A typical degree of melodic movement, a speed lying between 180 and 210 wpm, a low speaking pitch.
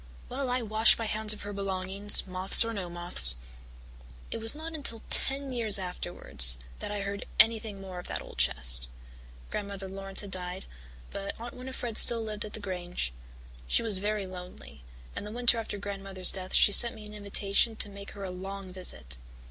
No: average, 3.0 semitones; average, 190 wpm; high, 200 Hz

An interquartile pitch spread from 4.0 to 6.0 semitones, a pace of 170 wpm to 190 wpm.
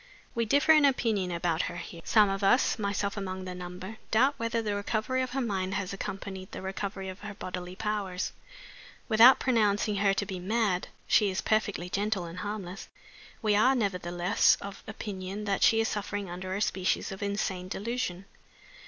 No: narrow, 2.6 semitones; average, 180 wpm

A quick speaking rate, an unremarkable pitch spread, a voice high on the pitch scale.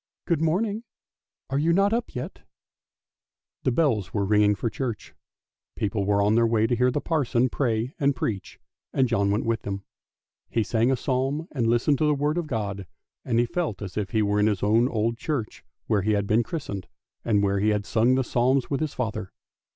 No: fast, 210 wpm; average, 4.8 semitones; low, 115 Hz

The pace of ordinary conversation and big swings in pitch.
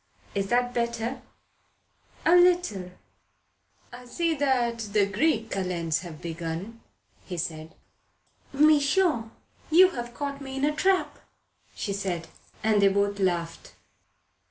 No: slow, 115 wpm; wide, 6.7 semitones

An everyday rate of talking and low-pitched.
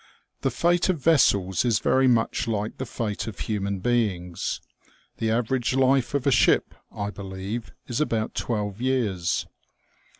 Yes: average, 145 wpm; low, 115 Hz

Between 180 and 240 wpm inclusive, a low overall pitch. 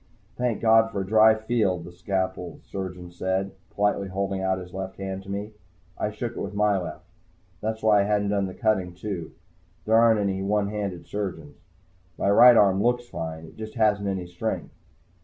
Yes: average, 190 wpm; low, 100 Hz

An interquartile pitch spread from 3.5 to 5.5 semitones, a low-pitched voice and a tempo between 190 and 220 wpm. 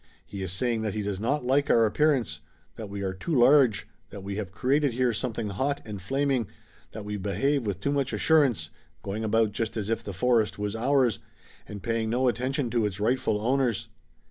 Yes: average, 4.2 semitones; low, 115 Hz; average, 200 wpm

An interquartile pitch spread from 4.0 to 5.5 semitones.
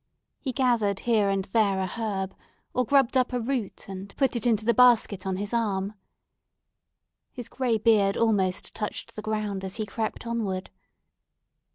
No: average, 3.2 semitones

